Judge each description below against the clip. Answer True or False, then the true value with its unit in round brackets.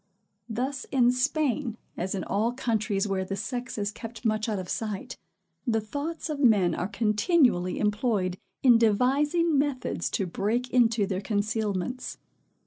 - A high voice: True (225 Hz)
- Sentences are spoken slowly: False (145 wpm)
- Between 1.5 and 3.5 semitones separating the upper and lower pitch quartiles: False (3.9 semitones)